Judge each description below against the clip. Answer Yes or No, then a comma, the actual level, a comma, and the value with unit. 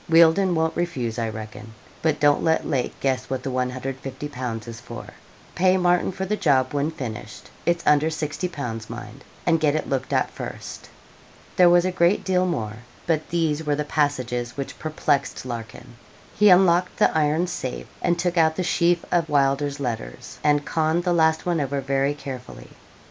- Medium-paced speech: Yes, average, 175 wpm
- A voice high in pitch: No, medium, 150 Hz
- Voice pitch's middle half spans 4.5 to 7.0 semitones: Yes, average, 4.9 semitones